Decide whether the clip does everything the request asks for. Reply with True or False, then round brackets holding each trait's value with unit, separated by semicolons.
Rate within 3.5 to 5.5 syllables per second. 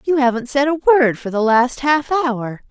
True (4.6 syllables/s)